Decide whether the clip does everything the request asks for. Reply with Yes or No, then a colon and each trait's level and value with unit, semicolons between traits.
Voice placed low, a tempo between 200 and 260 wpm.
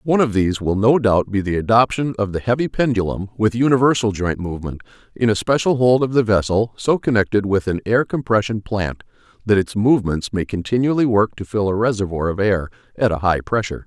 Yes: low, 110 Hz; fast, 205 wpm